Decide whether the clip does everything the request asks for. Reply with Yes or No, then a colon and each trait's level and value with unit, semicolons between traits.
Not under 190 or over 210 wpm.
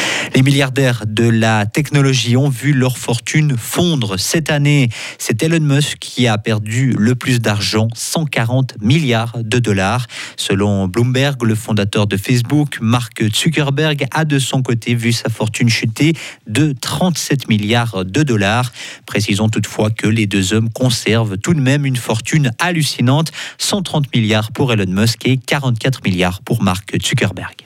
No: average, 150 wpm